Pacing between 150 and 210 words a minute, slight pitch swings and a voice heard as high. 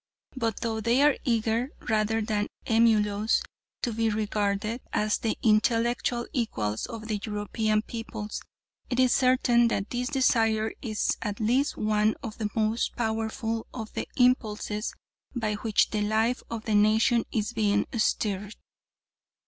No: average, 140 wpm; narrow, 1.7 semitones; high, 220 Hz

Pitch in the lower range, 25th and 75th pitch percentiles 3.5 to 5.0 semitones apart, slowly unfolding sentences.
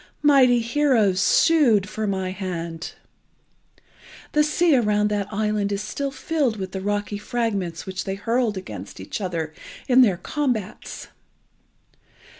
No: high, 210 Hz; average, 4.6 semitones; slow, 130 wpm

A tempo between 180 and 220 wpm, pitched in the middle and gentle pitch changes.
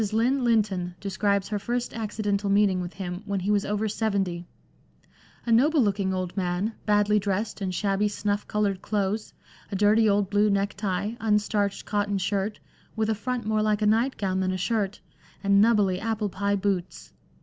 No: average, 185 wpm; high, 205 Hz; narrow, 1.8 semitones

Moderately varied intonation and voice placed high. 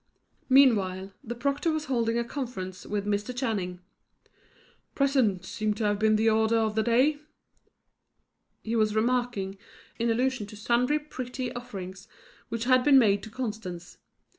Yes: average, 3.5 semitones; high, 225 Hz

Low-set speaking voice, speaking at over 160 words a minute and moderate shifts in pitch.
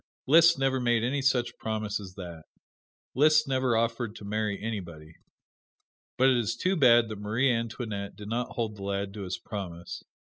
Yes: low, 115 Hz; average, 175 wpm; average, 3.9 semitones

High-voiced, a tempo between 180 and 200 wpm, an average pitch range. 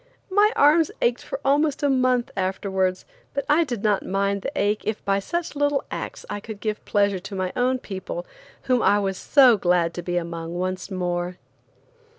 No: high, 205 Hz; average, 185 wpm; wide, 5.9 semitones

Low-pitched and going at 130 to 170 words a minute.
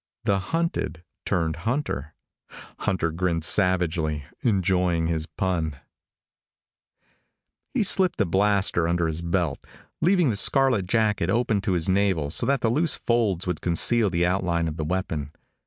Yes: very low, 90 Hz; average, 140 wpm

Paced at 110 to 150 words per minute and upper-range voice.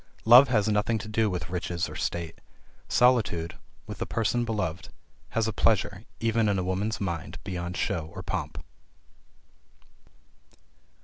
No: average, 140 wpm; low, 105 Hz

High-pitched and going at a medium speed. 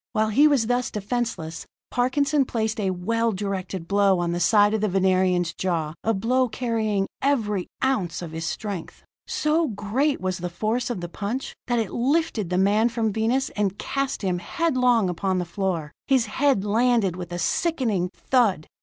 Yes: high, 210 Hz; average, 175 wpm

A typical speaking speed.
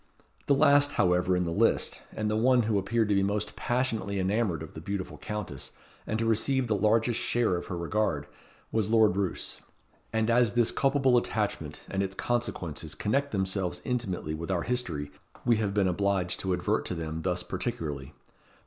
Yes: average, 180 wpm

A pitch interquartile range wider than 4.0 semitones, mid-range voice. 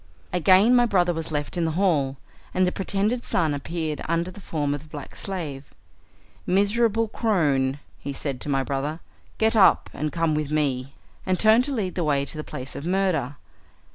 Yes: average, 5.1 semitones; medium, 165 Hz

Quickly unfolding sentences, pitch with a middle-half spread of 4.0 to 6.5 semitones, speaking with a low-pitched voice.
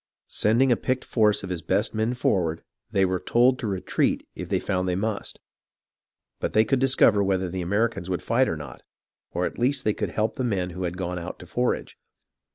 Yes: fast, 210 wpm; average, 4.5 semitones; low, 100 Hz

